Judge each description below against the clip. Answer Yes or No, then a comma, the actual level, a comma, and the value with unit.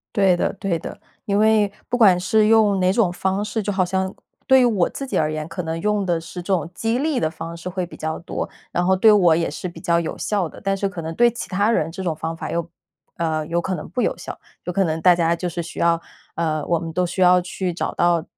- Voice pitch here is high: No, medium, 180 Hz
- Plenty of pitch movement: No, average, 3.2 semitones